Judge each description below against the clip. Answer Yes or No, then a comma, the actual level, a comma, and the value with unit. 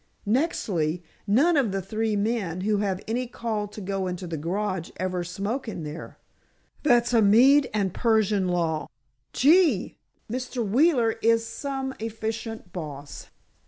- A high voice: Yes, high, 215 Hz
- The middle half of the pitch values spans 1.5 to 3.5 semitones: No, average, 4.4 semitones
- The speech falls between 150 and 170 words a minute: No, average, 140 wpm